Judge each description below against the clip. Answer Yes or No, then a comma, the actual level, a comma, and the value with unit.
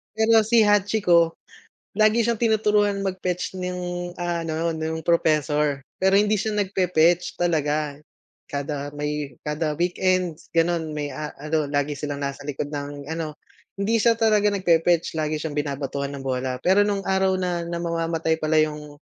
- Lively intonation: No, average, 4.2 semitones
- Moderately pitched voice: Yes, medium, 165 Hz